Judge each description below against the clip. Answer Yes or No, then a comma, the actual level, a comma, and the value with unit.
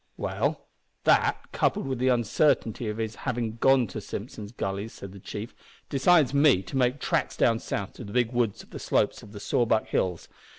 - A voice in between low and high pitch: No, low, 115 Hz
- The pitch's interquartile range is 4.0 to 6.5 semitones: No, average, 3.6 semitones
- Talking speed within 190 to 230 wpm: Yes, average, 195 wpm